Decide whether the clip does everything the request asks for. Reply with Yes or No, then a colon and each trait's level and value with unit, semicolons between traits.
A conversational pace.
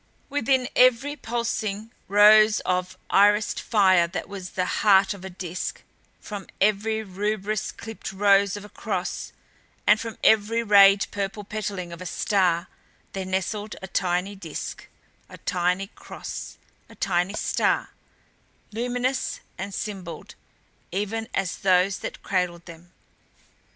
No: slow, 130 wpm